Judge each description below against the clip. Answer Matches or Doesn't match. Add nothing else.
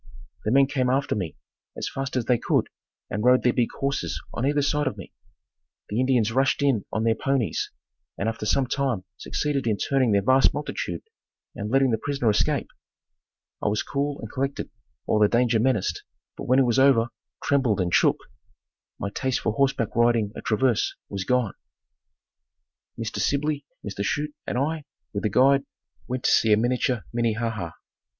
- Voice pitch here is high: Doesn't match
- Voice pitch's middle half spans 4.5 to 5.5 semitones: Doesn't match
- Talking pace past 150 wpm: Matches